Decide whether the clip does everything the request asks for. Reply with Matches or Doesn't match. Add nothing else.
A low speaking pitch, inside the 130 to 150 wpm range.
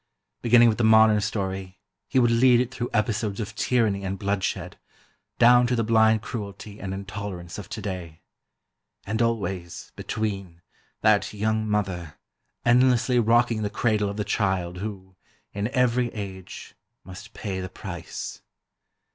Matches